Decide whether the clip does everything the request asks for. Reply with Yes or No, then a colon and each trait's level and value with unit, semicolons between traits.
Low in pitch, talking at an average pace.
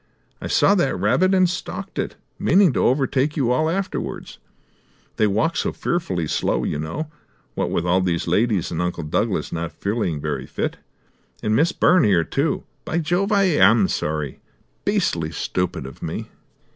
Yes: low, 110 Hz; average, 165 wpm